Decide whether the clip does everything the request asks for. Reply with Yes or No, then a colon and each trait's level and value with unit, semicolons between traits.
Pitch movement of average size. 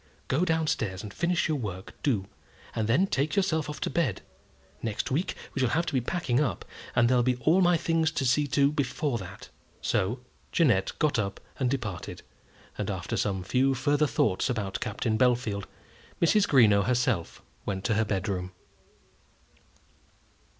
No: wide, 6.3 semitones